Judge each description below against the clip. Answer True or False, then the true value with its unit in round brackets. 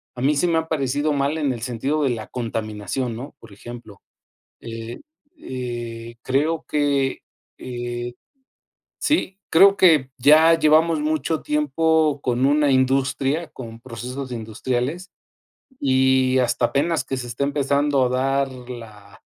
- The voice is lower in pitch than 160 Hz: True (135 Hz)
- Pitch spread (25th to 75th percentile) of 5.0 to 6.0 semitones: False (3.6 semitones)